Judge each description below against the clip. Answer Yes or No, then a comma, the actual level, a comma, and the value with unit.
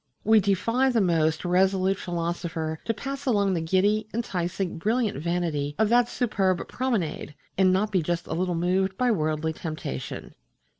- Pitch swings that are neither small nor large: Yes, average, 4.2 semitones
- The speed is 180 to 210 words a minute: No, average, 155 wpm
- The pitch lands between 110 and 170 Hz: No, medium, 185 Hz